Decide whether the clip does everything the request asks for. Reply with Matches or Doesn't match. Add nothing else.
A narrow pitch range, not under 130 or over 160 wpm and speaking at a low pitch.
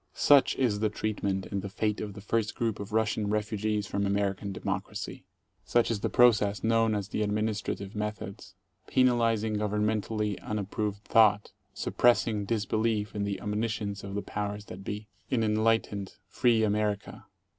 Matches